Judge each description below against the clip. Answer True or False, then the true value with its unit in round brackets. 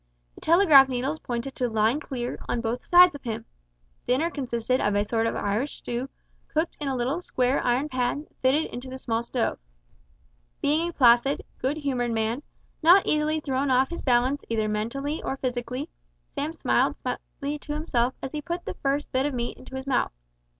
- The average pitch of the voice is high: True (260 Hz)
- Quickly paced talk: False (190 wpm)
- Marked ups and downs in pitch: False (3.5 semitones)